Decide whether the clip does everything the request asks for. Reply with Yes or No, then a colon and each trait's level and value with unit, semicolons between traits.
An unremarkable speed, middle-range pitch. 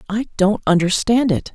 No: average, 155 wpm; high, 205 Hz